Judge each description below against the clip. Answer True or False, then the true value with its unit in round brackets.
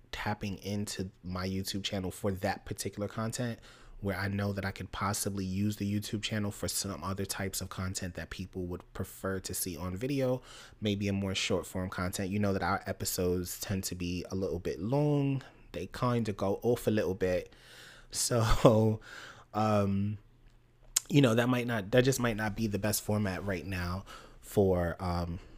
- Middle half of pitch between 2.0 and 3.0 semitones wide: True (2.5 semitones)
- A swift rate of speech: False (185 wpm)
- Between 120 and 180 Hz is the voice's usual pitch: False (100 Hz)